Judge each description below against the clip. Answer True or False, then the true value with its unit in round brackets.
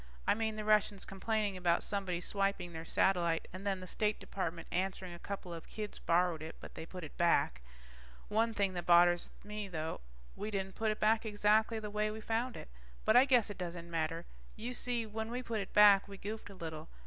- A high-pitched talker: True (200 Hz)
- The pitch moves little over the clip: False (3.6 semitones)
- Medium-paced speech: False (215 wpm)